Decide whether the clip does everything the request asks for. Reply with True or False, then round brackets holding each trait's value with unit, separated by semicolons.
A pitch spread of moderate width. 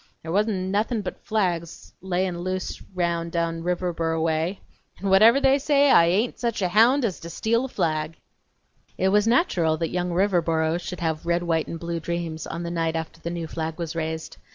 True (3.3 semitones)